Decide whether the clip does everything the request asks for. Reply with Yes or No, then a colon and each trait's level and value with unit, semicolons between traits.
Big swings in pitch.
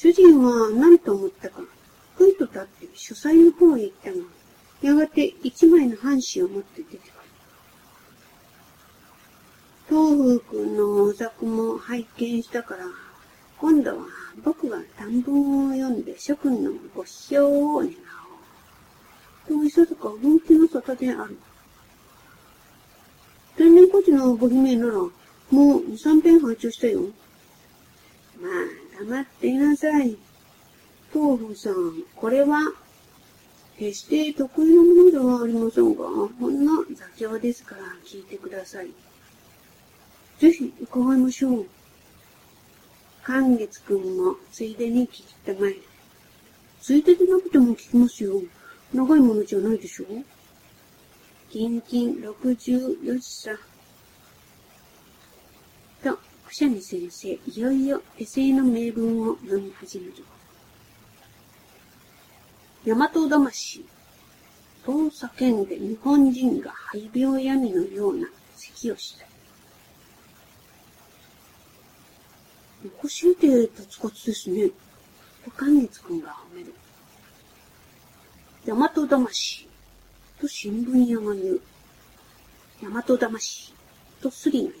Yes: wide, 5.9 semitones